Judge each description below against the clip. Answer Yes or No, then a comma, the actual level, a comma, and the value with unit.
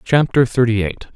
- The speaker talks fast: No, average, 155 wpm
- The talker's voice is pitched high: No, low, 120 Hz